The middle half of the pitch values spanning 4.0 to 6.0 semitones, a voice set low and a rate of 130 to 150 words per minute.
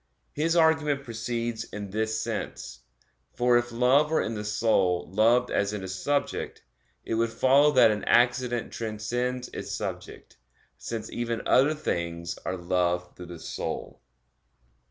No: average, 3.5 semitones; low, 115 Hz; average, 145 wpm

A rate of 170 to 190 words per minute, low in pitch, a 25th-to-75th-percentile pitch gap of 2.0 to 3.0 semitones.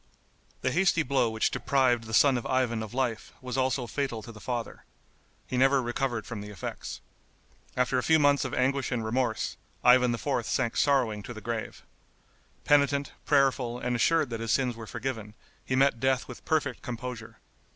Yes: average, 180 wpm; low, 125 Hz; average, 2.7 semitones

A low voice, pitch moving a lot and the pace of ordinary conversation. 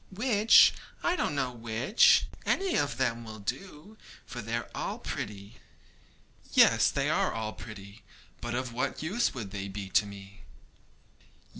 Yes: low, 120 Hz; wide, 6.0 semitones; average, 150 wpm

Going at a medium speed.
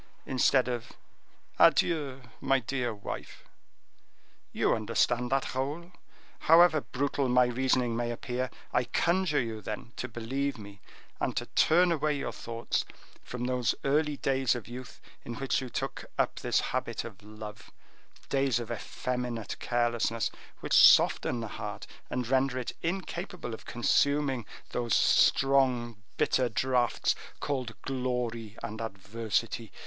No: slow, 130 wpm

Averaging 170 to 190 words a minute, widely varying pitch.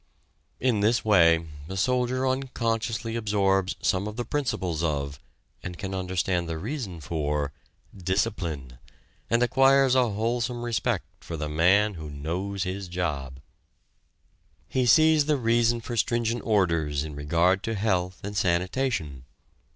No: slow, 135 wpm; wide, 5.9 semitones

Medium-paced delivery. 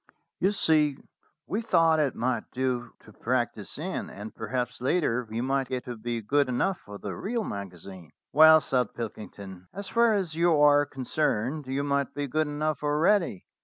Yes: average, 175 wpm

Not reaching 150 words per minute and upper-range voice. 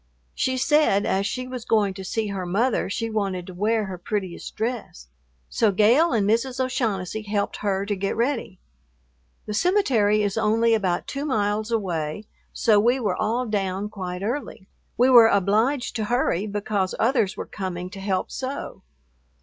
No: average, 165 wpm; high, 210 Hz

